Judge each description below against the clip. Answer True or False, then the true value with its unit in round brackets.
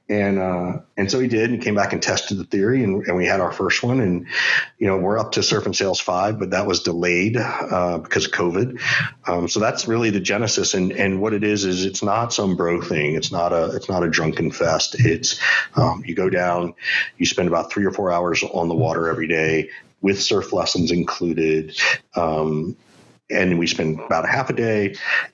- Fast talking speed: True (220 wpm)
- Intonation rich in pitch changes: False (3.3 semitones)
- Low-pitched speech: True (90 Hz)